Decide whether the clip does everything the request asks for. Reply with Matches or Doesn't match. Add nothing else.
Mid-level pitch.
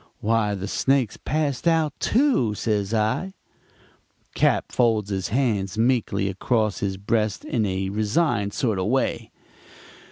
Doesn't match